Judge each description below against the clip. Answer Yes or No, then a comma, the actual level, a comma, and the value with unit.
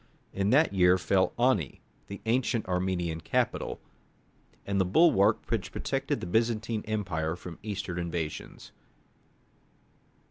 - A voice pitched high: No, very low, 95 Hz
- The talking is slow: Yes, slow, 115 wpm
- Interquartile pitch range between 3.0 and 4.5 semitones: Yes, average, 3.8 semitones